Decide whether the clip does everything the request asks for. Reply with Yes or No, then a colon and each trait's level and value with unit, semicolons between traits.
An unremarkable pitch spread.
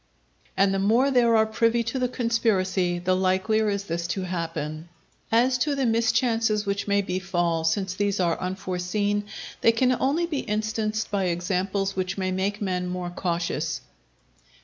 Yes: average, 3.6 semitones